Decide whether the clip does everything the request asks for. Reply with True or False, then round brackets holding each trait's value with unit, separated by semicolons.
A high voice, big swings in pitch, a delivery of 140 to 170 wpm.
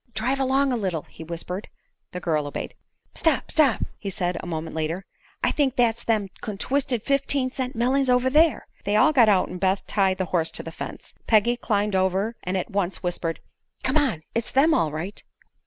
False (210 Hz; 6.3 semitones; 195 wpm)